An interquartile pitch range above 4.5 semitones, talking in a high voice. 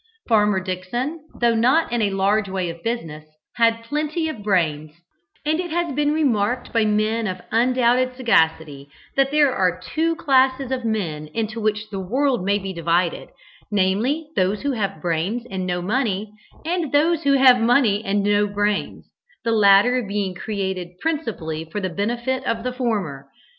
Yes: average, 5.2 semitones; high, 215 Hz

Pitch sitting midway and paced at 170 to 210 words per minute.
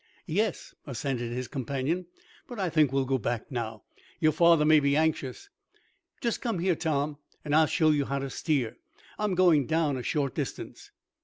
Yes: medium, 150 Hz; average, 175 wpm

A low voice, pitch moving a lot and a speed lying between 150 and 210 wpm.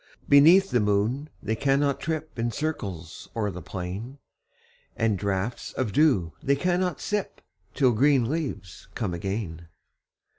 No: low, 120 Hz; wide, 6.8 semitones; slow, 135 wpm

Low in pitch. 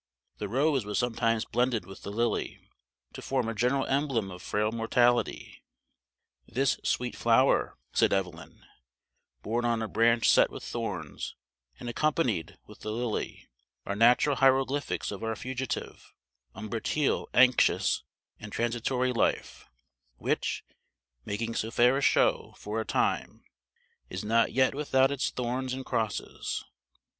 Yes: low, 120 Hz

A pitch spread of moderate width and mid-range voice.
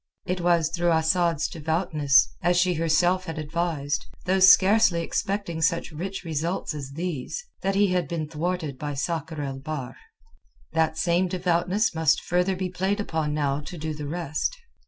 Yes: average, 3.0 semitones; medium, 170 Hz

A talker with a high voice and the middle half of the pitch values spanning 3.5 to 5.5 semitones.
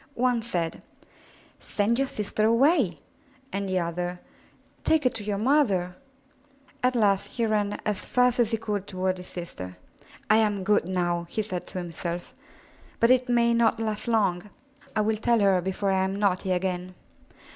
Yes: high, 205 Hz; average, 4.0 semitones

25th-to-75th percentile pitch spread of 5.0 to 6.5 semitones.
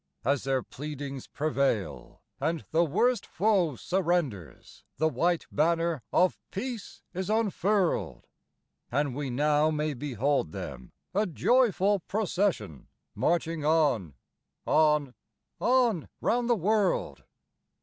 Yes: wide, 5.4 semitones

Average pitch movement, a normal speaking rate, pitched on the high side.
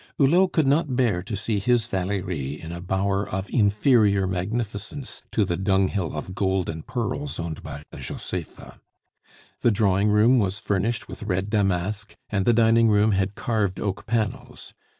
No: average, 3.3 semitones; average, 165 wpm; low, 100 Hz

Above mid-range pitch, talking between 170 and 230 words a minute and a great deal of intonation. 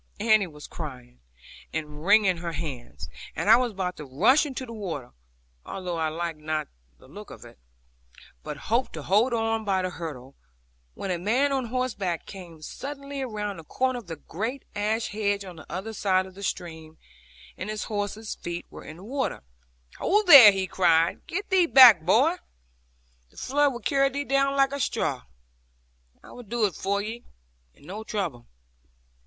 Yes: high, 200 Hz; average, 180 wpm; wide, 6.7 semitones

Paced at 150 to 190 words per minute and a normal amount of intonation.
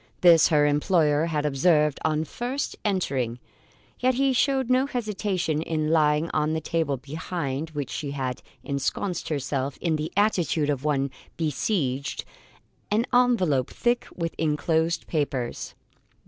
No: slow, 135 wpm; average, 4.2 semitones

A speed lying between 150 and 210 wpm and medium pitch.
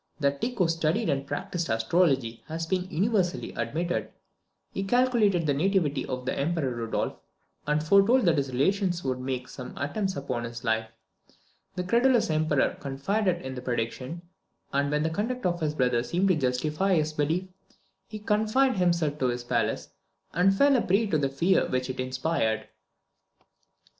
Yes: average, 165 wpm; medium, 155 Hz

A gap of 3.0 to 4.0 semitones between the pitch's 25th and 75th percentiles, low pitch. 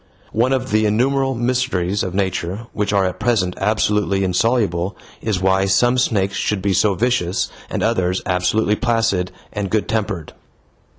Yes: average, 3.6 semitones; low, 105 Hz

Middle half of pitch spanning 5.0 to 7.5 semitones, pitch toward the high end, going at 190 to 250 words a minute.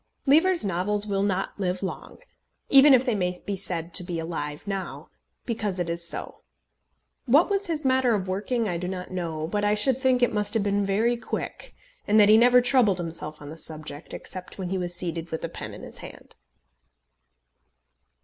Yes: average, 5.3 semitones; high, 200 Hz; average, 195 wpm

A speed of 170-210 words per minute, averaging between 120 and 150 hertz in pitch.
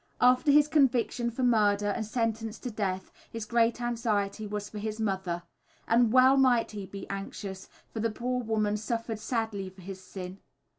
No: average, 175 wpm; high, 220 Hz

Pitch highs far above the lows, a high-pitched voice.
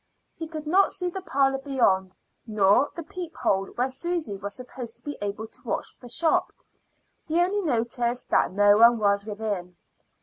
Yes: wide, 7.4 semitones; high, 240 Hz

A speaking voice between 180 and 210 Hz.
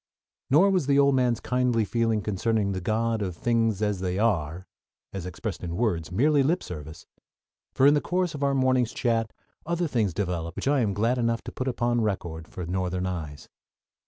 No: low, 115 Hz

